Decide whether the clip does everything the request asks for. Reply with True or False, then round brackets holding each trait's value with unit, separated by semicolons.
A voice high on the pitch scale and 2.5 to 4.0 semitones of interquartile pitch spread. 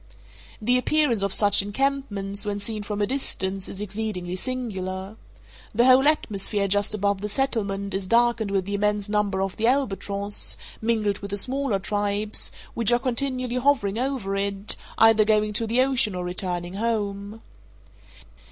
True (210 Hz; 3.1 semitones)